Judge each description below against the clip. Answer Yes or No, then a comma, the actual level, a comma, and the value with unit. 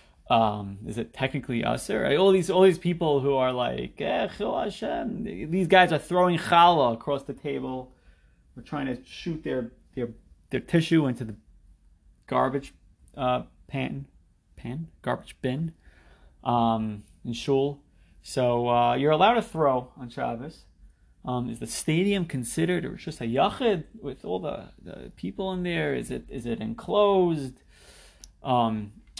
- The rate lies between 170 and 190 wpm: No, average, 150 wpm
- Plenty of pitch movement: Yes, wide, 6.7 semitones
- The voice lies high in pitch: No, low, 130 Hz